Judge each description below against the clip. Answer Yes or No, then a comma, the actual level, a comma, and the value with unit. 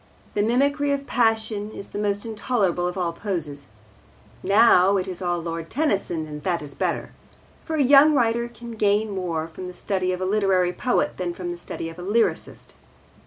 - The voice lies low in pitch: No, high, 195 Hz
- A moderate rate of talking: Yes, average, 190 wpm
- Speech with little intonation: No, average, 4.5 semitones